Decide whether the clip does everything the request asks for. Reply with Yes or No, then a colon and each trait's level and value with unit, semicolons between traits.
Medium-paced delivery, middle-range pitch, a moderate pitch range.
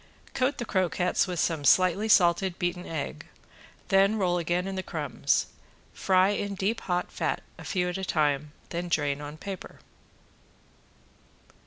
No: average, 150 wpm; medium, 180 Hz; narrow, 2.3 semitones